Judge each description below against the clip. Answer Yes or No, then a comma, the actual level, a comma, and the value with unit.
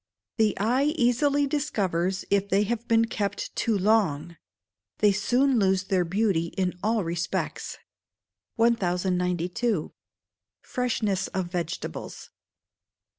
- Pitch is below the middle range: No, high, 200 Hz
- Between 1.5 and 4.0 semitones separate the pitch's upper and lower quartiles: No, average, 4.4 semitones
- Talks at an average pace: No, slow, 105 wpm